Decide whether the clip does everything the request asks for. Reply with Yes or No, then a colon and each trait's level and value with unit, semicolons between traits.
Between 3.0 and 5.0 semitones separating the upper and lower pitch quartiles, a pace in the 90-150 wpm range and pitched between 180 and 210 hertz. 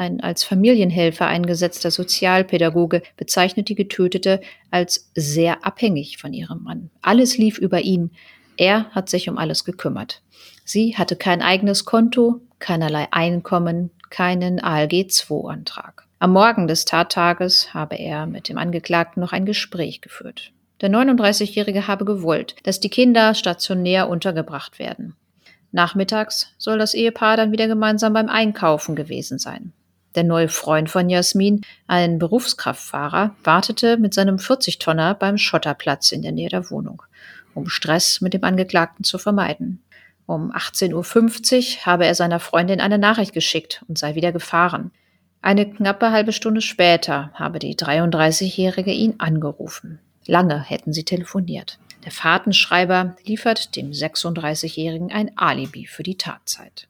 Yes: average, 3.6 semitones; average, 140 wpm; medium, 185 Hz